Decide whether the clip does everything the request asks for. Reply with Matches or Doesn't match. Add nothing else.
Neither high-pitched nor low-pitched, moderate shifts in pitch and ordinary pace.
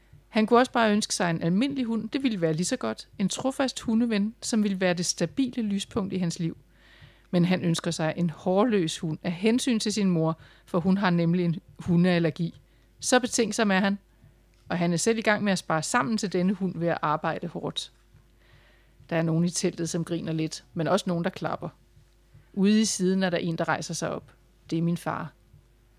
Matches